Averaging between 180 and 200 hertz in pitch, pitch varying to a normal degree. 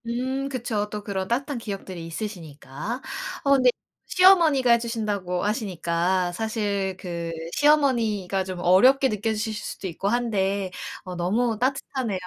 No: high, 210 Hz; average, 4.7 semitones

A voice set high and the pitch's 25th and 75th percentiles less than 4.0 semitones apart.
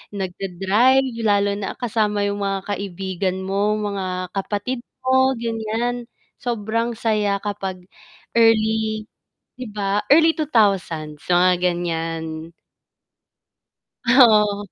Yes: high, 205 Hz; average, 3.2 semitones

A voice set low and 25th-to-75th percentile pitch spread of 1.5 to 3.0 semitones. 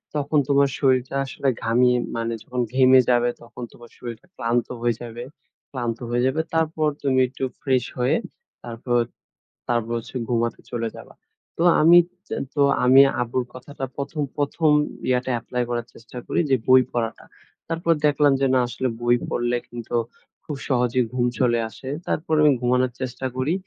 Yes: low, 125 Hz; narrow, 2.4 semitones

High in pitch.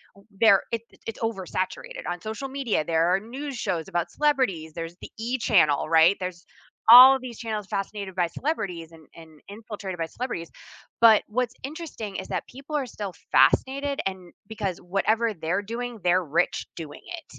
Yes: high, 205 Hz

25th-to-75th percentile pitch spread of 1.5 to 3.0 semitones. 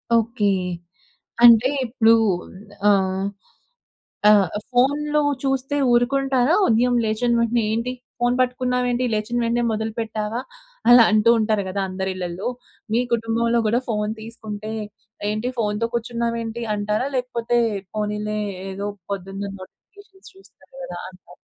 Yes: average, 2.7 semitones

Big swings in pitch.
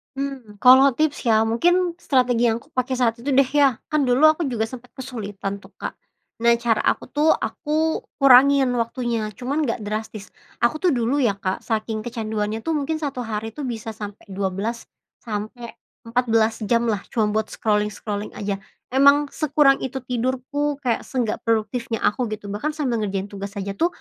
No: average, 4.0 semitones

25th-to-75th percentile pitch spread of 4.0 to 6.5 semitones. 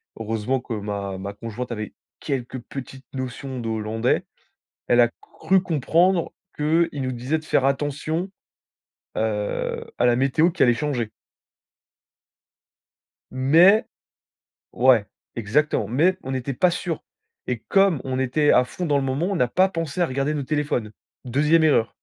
Yes: average, 4.7 semitones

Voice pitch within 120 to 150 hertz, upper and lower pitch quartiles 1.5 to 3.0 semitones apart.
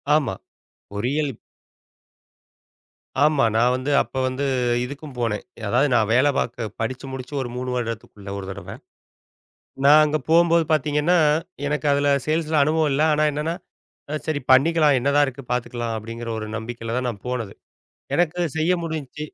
No: low, 135 Hz; average, 4.2 semitones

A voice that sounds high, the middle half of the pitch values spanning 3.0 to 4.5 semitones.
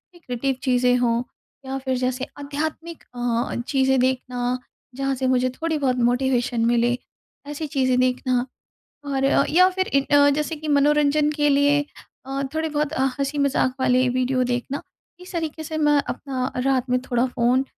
No: very high, 265 Hz; narrow, 2.6 semitones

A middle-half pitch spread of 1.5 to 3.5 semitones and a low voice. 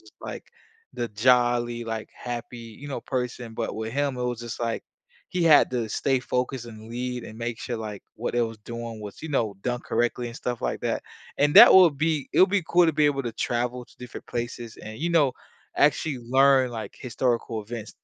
Yes: narrow, 2.5 semitones; low, 120 Hz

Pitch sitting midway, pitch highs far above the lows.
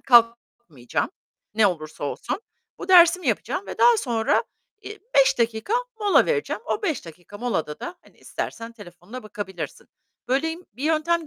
No: high, 240 Hz; wide, 9.0 semitones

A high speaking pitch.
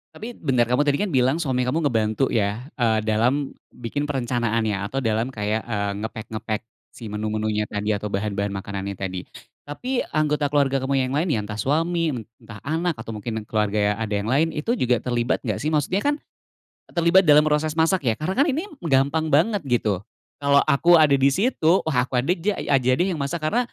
No: low, 130 Hz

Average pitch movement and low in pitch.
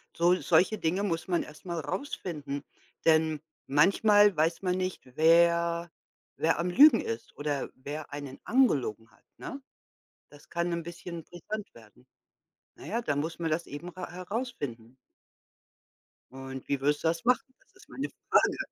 No: average, 3.9 semitones; medium, 165 Hz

